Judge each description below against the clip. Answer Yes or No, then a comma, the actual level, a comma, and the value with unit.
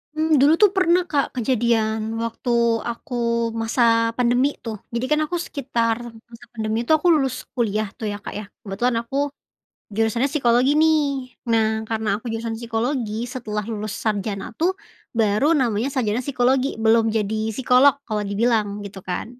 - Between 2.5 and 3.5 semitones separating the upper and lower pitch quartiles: Yes, average, 3.1 semitones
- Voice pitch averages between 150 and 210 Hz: No, high, 235 Hz